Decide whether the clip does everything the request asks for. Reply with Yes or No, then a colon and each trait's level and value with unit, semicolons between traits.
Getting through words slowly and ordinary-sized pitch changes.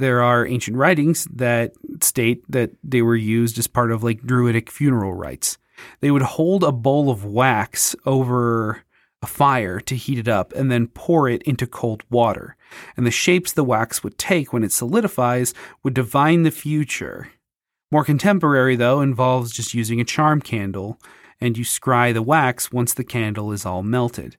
No: average, 175 wpm; average, 3.3 semitones